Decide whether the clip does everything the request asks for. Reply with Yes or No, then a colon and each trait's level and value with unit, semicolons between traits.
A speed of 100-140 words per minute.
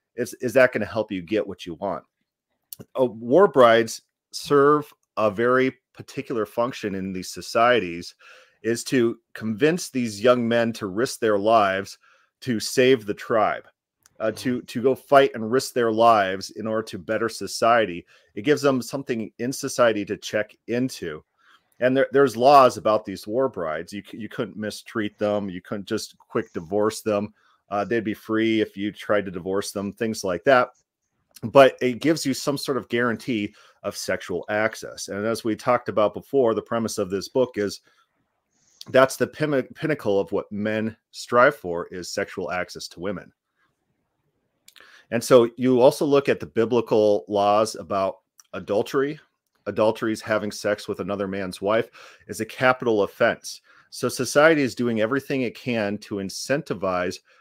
No: average, 165 wpm